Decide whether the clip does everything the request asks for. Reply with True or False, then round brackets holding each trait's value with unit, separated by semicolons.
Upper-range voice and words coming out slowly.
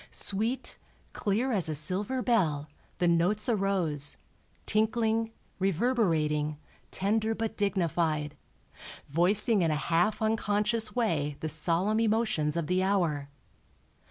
True (195 Hz; 110 wpm)